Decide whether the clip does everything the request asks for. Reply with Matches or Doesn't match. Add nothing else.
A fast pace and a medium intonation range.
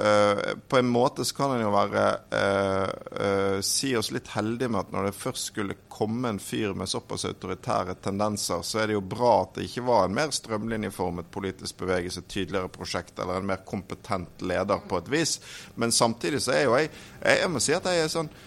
Matches